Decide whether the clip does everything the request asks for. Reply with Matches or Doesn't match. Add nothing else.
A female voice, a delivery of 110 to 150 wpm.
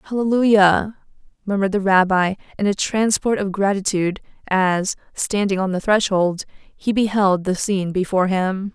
Matches